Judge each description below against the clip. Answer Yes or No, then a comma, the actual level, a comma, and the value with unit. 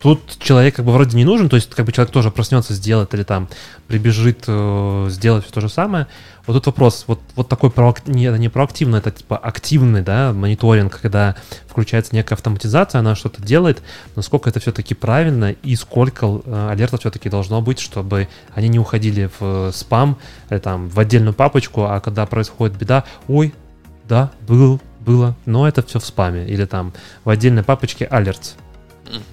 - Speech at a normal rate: No, fast, 180 wpm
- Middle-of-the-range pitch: No, low, 115 Hz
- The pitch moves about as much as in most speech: Yes, average, 3.5 semitones